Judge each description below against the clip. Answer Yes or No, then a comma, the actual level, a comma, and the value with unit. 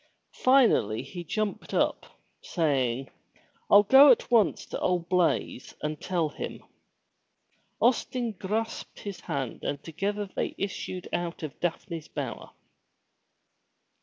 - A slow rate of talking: Yes, slow, 120 wpm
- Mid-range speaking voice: Yes, medium, 180 Hz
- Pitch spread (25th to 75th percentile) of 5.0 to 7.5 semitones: Yes, wide, 5.4 semitones